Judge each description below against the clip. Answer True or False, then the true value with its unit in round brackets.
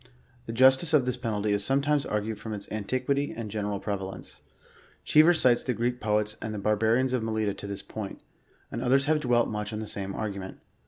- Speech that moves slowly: False (205 wpm)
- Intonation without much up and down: False (3.7 semitones)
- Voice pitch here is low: True (110 Hz)